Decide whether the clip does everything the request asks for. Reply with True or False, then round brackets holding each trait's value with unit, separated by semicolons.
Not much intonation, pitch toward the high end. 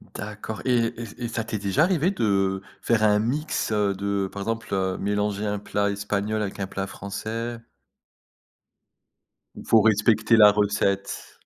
False (2.2 semitones; 105 Hz)